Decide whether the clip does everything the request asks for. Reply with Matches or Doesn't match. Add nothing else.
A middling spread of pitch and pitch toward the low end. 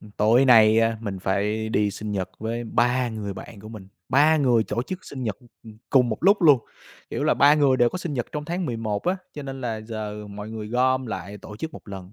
Matches